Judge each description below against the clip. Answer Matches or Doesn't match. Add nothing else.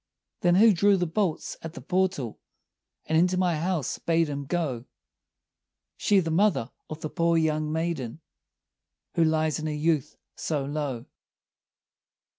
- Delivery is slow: Doesn't match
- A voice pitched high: Doesn't match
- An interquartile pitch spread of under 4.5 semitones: Matches